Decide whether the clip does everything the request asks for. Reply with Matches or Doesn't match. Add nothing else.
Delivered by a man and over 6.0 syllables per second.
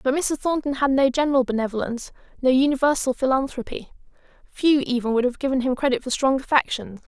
Doesn't match